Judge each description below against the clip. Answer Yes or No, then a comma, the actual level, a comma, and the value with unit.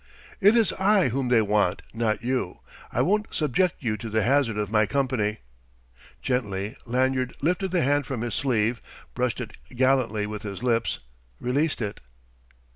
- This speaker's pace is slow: No, average, 160 wpm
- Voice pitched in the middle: No, low, 125 Hz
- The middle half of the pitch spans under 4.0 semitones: No, average, 4.3 semitones